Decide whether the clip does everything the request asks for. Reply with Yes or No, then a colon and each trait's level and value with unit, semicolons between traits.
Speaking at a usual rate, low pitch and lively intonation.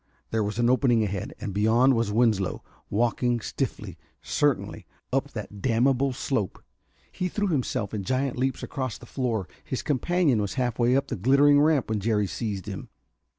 No: average, 170 wpm; low, 120 Hz; average, 3.8 semitones